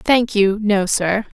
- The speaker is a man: No, female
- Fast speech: No, average, 175 wpm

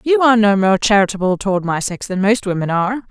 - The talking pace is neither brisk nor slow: No, fast, 230 wpm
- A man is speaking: No, female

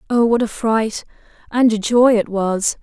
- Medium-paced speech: Yes, average, 190 wpm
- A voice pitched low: No, high, 225 Hz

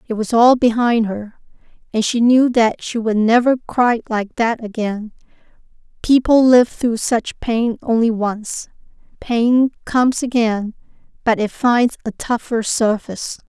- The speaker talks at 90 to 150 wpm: Yes, average, 140 wpm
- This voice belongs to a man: No, female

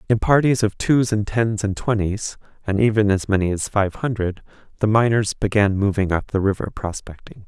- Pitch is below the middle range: Yes, low, 105 Hz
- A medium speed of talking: Yes, average, 185 wpm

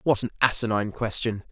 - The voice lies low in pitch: Yes, low, 110 Hz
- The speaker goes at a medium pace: Yes, average, 160 wpm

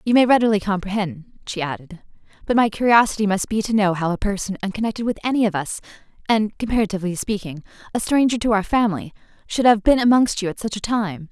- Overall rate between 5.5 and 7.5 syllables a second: Yes, 6.1 syllables/s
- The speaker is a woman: Yes, female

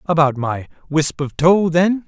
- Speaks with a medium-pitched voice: Yes, medium, 160 Hz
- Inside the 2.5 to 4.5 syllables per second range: Yes, 4.1 syllables/s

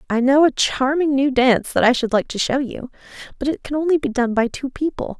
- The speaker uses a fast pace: Yes, fast, 255 wpm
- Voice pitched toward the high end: Yes, very high, 265 Hz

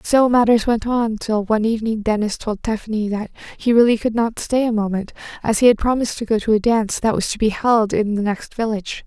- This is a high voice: Yes, high, 220 Hz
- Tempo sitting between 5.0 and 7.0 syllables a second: Yes, 5.9 syllables/s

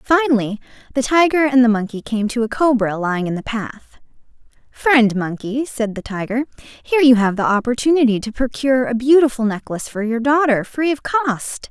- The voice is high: Yes, high, 245 Hz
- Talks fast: No, average, 180 wpm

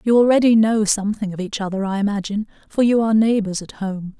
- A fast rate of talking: Yes, fast, 215 wpm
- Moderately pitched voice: No, high, 210 Hz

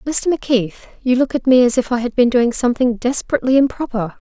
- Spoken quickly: Yes, fast, 210 wpm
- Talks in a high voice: Yes, very high, 250 Hz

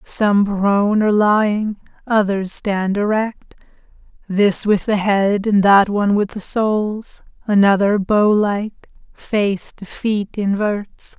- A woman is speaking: Yes, female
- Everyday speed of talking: No, slow, 130 wpm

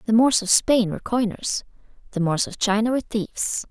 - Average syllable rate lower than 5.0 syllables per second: No, 5.6 syllables/s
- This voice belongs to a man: No, female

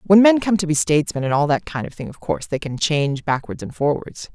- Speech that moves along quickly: Yes, fast, 275 wpm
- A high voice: No, medium, 160 Hz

